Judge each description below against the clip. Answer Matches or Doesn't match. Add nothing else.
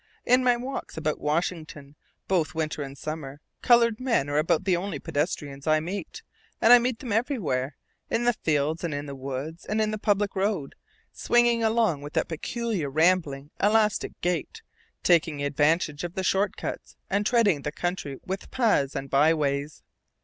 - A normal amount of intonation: Doesn't match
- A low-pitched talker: Doesn't match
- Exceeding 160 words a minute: Matches